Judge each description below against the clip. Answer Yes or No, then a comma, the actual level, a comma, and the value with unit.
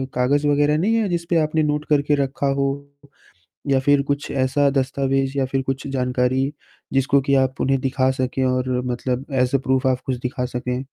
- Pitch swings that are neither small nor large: No, narrow, 1.7 semitones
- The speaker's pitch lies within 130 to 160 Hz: Yes, low, 135 Hz